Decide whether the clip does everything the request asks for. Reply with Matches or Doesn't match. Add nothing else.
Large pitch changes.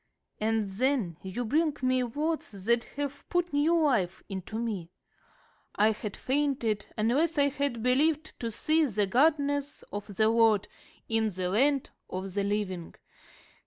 Matches